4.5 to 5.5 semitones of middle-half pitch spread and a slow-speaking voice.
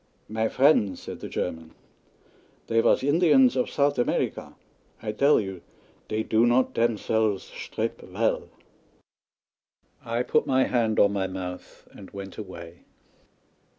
Yes: average, 4.9 semitones; slow, 130 wpm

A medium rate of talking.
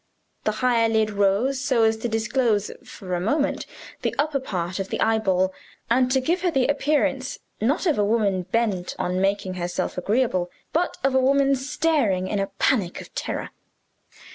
Yes: average, 175 wpm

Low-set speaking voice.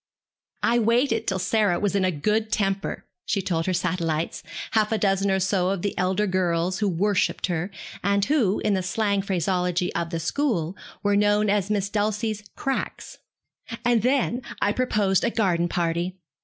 No: high, 195 Hz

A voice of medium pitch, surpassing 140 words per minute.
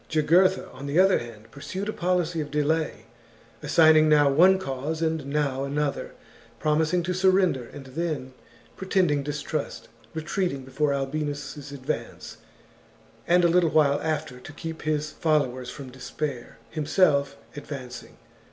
No: medium, 150 Hz; slow, 135 wpm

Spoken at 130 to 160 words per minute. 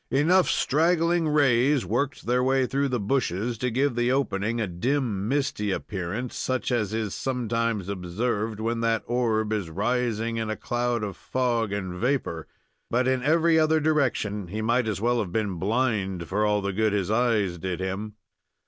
No: average, 175 wpm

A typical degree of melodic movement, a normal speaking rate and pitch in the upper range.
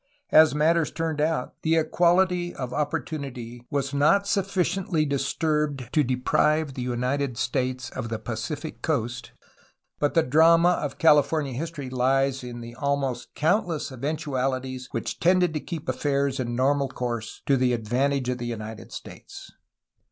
No: average, 3.9 semitones; average, 150 wpm; medium, 140 Hz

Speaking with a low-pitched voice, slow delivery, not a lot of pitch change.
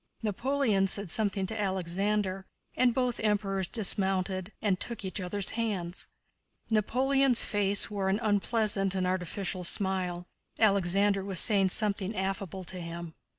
No: high, 195 Hz; slow, 130 wpm; narrow, 2.2 semitones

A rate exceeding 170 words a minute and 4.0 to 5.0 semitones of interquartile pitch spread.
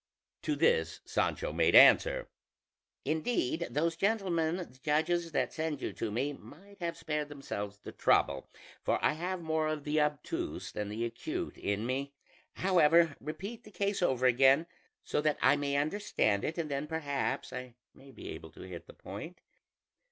No: average, 165 wpm; average, 4.7 semitones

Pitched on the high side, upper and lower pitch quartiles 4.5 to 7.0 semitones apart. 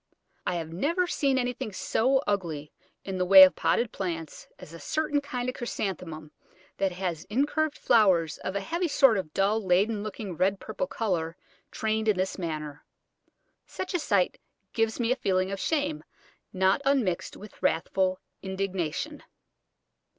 Yes: high, 195 Hz; average, 5.3 semitones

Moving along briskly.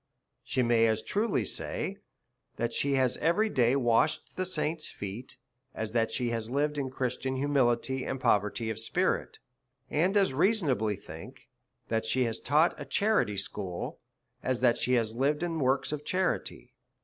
No: average, 165 wpm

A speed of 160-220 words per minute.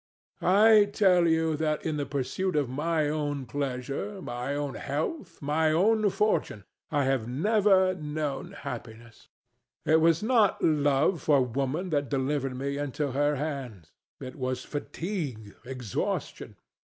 No: slow, 135 wpm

